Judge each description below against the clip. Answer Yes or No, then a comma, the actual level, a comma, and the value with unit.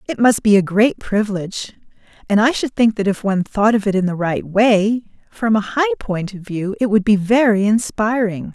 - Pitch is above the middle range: Yes, high, 205 Hz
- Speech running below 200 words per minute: No, fast, 205 wpm